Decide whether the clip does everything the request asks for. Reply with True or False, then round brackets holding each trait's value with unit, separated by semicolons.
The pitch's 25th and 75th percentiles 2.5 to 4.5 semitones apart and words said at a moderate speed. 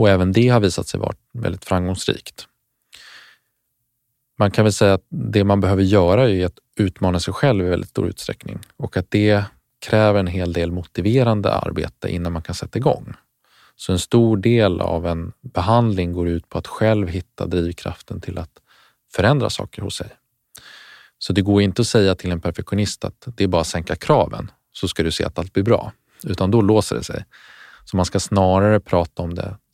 True (3.5 semitones; 195 wpm)